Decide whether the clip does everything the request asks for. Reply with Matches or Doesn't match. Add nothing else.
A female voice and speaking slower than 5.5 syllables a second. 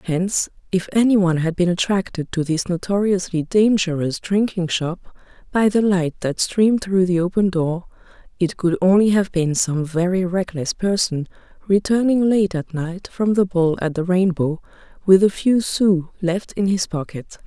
Matches